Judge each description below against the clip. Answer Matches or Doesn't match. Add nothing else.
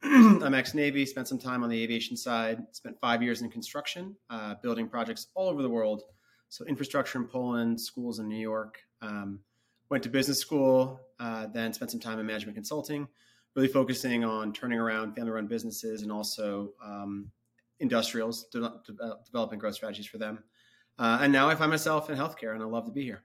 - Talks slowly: Doesn't match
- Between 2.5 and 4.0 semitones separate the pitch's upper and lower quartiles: Matches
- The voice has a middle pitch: Doesn't match